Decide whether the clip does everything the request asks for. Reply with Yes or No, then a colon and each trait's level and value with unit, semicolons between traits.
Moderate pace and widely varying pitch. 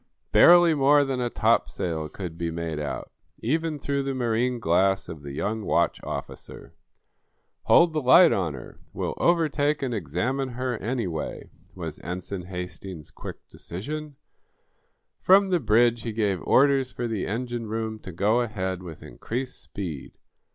Yes: average, 150 wpm; wide, 6.9 semitones